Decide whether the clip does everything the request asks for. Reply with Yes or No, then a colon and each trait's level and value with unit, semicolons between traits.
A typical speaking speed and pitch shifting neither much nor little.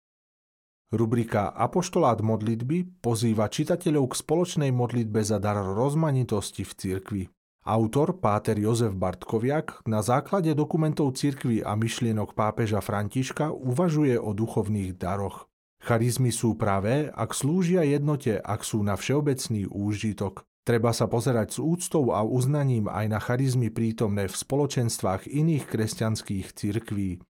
Yes: average, 125 wpm; average, 4.9 semitones